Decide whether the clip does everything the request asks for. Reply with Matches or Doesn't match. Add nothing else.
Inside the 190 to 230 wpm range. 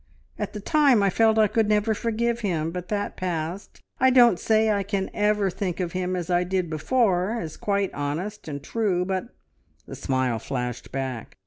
Matches